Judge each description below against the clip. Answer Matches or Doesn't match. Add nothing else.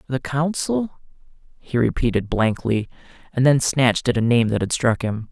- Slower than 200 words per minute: Matches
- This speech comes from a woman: Doesn't match